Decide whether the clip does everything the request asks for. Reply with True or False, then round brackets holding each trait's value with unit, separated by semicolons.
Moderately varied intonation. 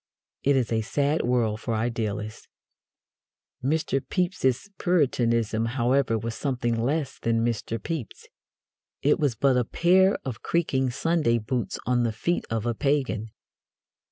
True (3.8 semitones)